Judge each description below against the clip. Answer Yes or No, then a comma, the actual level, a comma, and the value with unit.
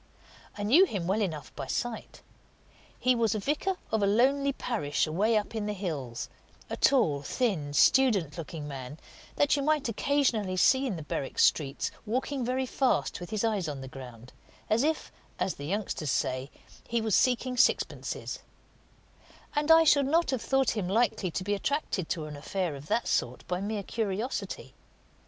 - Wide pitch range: Yes, wide, 8.3 semitones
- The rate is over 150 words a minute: Yes, average, 175 wpm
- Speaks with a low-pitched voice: No, high, 210 Hz